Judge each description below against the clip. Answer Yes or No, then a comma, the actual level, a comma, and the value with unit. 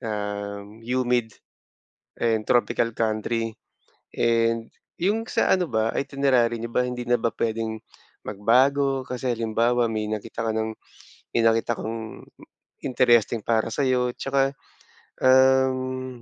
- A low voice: Yes, low, 115 Hz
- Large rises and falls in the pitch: No, narrow, 2.5 semitones